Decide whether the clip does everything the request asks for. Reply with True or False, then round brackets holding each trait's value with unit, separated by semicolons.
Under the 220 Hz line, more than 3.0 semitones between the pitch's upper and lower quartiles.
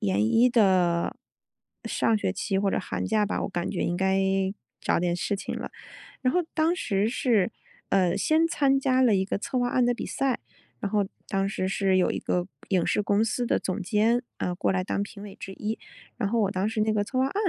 True (205 Hz; 4.1 semitones)